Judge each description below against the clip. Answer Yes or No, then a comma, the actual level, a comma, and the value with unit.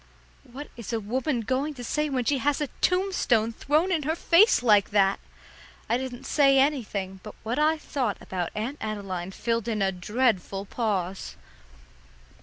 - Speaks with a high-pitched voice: Yes, high, 240 Hz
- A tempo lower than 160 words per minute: No, average, 165 wpm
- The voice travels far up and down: Yes, wide, 5.8 semitones